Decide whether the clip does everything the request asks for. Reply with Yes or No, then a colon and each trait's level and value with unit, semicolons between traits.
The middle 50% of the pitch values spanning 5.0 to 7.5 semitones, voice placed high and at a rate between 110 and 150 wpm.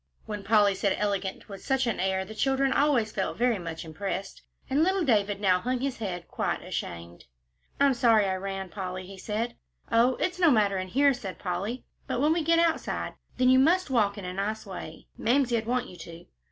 No: average, 5.3 semitones; high, 215 Hz; fast, 205 wpm